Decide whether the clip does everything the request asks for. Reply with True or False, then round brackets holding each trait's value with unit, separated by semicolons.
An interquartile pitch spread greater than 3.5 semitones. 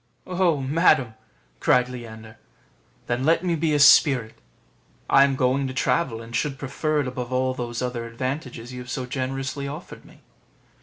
False (2.8 semitones)